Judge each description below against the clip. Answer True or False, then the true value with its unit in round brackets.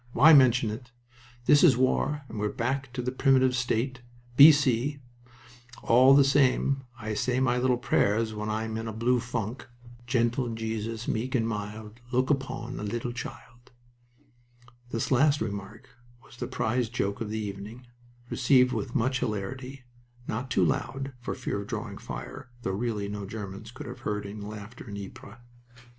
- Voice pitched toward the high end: False (120 Hz)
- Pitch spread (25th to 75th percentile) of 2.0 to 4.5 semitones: True (3.1 semitones)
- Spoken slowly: False (165 wpm)